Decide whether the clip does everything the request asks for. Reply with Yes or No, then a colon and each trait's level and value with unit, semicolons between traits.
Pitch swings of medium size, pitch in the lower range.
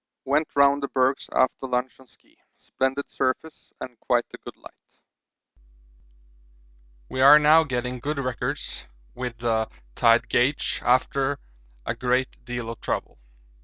No: narrow, 2.2 semitones; low, 130 Hz